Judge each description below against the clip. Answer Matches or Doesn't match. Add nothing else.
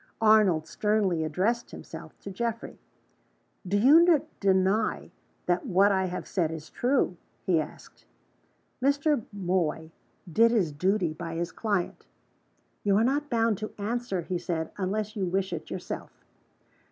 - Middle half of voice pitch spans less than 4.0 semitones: Doesn't match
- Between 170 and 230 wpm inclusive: Doesn't match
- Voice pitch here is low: Doesn't match